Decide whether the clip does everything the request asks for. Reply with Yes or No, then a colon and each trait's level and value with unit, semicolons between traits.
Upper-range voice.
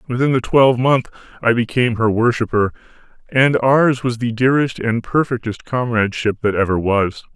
No: low, 120 Hz